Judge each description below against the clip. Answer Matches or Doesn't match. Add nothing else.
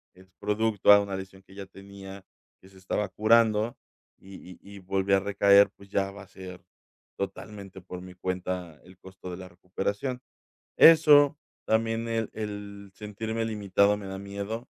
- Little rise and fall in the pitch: Matches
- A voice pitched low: Matches